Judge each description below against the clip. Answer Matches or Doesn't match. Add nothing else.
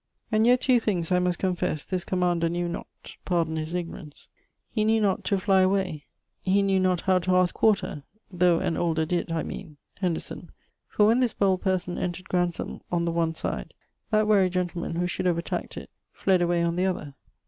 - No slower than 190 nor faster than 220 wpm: Matches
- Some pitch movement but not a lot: Doesn't match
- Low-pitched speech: Doesn't match